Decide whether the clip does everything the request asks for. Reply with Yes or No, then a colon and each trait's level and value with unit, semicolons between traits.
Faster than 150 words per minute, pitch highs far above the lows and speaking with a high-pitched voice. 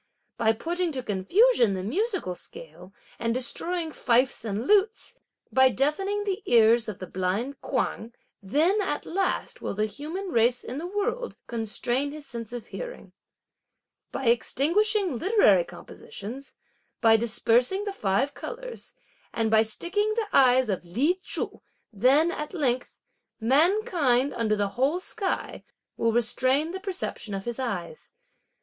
No: average, 140 wpm; wide, 8.7 semitones; very high, 265 Hz